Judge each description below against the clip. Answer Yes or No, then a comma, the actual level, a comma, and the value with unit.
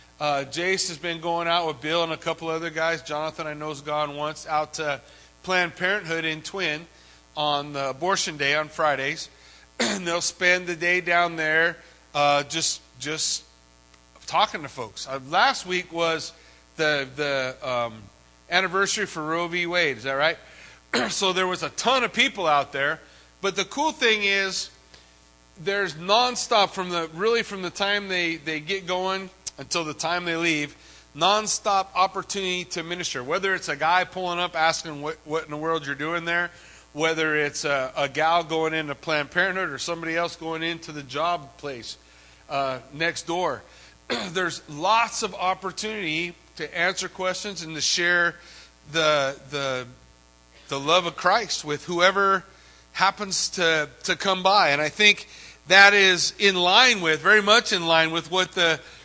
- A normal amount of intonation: Yes, average, 3.9 semitones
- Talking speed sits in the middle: Yes, average, 170 wpm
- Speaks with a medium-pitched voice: Yes, medium, 165 Hz